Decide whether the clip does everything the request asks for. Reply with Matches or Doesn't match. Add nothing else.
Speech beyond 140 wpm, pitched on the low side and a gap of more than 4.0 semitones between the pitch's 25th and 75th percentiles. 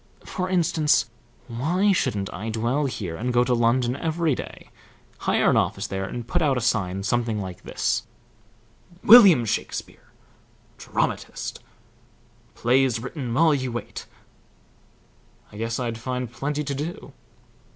Doesn't match